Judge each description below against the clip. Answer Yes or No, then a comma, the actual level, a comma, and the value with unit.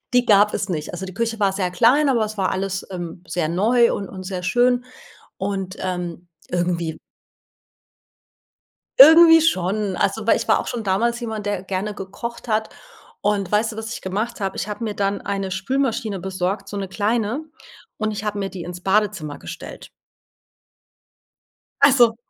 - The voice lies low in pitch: No, high, 200 Hz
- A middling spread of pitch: Yes, average, 3.2 semitones